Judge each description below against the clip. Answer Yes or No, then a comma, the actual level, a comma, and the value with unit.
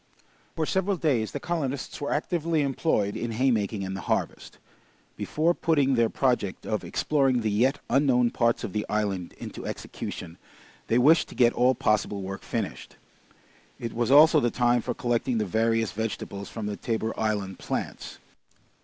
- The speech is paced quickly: No, average, 160 wpm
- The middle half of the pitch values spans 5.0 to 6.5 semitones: No, average, 4.5 semitones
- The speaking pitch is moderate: No, low, 120 Hz